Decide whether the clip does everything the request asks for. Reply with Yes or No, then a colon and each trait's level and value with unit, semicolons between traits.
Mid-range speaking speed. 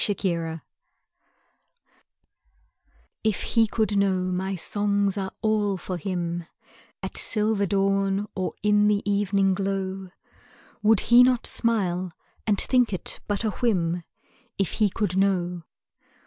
No: slow, 120 wpm